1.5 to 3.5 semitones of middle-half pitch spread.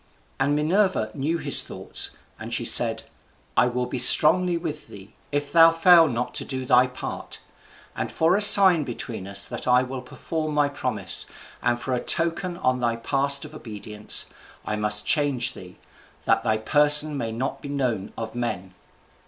No: average, 4.9 semitones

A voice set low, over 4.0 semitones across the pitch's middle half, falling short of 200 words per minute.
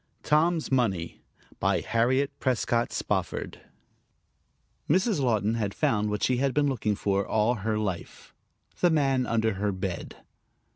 Yes: low, 115 Hz; average, 4.5 semitones; slow, 135 wpm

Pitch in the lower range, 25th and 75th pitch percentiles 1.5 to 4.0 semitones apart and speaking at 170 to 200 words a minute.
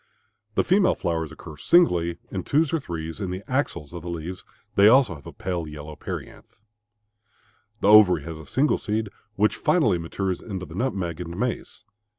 No: very low, 90 Hz; average, 4.7 semitones; average, 175 wpm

